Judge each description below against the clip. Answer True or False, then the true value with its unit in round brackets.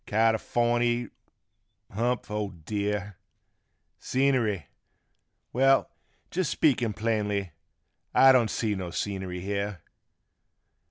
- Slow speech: True (85 wpm)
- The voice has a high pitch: False (105 Hz)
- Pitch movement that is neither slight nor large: True (3.2 semitones)